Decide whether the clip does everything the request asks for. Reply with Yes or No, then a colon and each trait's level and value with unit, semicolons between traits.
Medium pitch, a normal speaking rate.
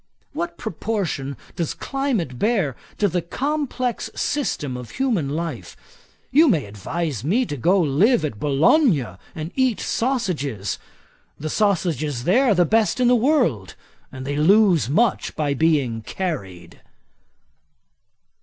No: medium, 170 Hz; slow, 130 wpm